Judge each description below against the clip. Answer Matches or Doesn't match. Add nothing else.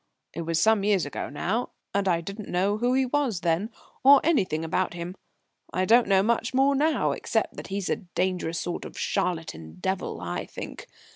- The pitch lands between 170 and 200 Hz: Matches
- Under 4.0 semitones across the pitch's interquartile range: Doesn't match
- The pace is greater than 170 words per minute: Matches